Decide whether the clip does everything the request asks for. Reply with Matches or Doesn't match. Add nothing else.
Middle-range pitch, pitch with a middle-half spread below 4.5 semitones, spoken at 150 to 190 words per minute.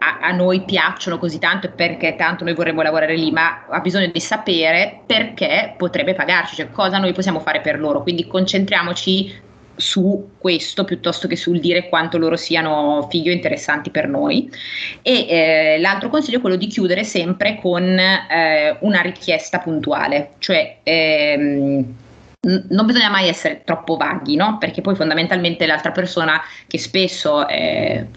Matches